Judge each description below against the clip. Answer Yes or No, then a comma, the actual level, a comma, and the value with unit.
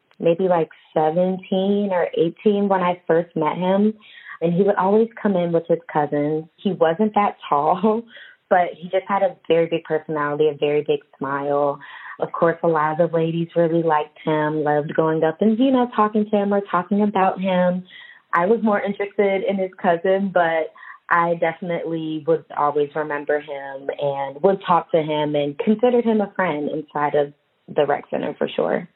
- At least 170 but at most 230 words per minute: Yes, average, 185 wpm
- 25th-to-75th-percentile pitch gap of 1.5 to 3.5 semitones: No, average, 4.3 semitones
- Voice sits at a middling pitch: Yes, medium, 170 Hz